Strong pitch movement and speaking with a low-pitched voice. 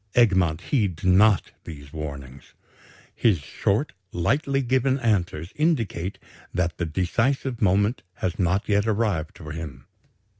Yes: wide, 5.8 semitones; very low, 95 Hz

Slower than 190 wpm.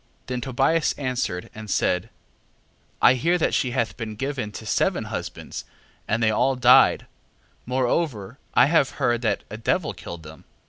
Yes: average, 165 wpm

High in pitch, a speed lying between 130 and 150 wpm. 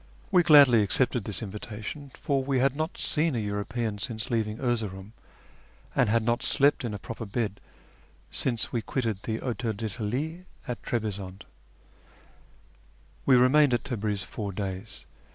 No: low, 115 Hz; average, 145 wpm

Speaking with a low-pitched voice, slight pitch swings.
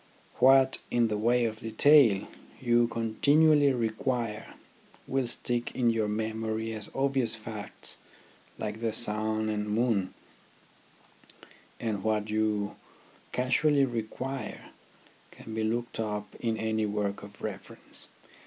Yes: low, 110 Hz; narrow, 2.2 semitones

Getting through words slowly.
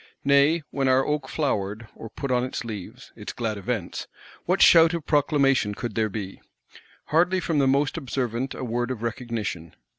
No: average, 175 wpm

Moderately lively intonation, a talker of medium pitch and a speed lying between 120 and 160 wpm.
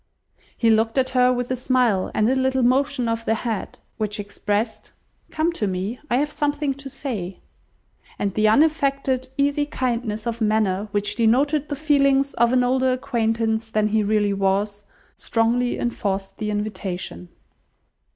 No: average, 3.8 semitones; high, 235 Hz; average, 155 wpm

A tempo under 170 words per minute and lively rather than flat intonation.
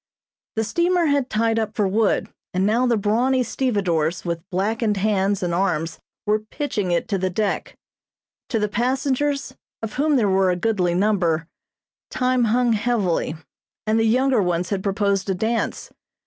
No: average, 160 wpm; average, 4.2 semitones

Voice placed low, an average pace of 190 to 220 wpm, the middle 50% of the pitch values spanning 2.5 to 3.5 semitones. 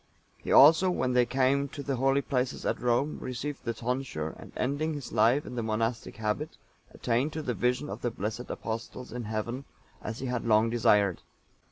Yes: low, 125 Hz; average, 195 wpm; average, 3.2 semitones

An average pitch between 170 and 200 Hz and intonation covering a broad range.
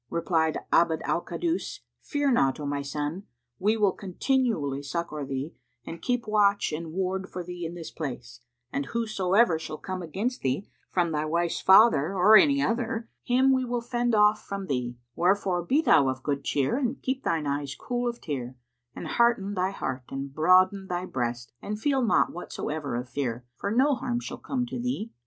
Yes: medium, 185 Hz; wide, 7.9 semitones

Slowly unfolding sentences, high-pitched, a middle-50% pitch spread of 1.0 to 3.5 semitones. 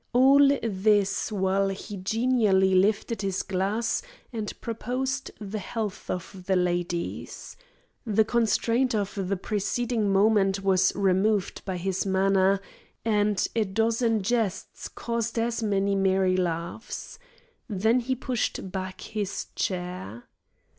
Yes: slow, 120 wpm; high, 200 Hz; average, 3.1 semitones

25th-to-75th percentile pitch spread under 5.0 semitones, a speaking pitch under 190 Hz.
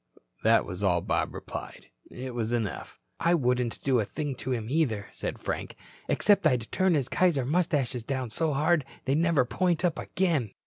No: wide, 5.6 semitones; low, 135 Hz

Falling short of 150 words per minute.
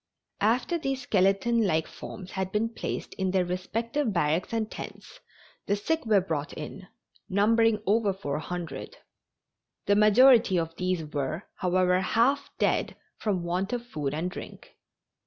Yes: average, 140 wpm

